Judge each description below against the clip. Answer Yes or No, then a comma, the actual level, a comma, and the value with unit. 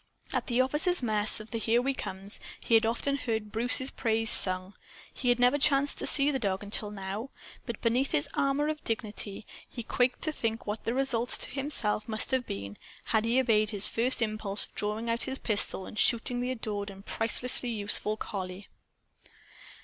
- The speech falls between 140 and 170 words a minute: No, average, 190 wpm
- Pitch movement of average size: Yes, average, 3.5 semitones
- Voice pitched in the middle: No, high, 225 Hz